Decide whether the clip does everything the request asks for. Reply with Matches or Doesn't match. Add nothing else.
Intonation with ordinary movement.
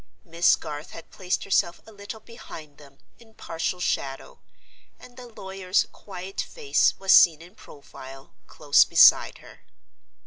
Matches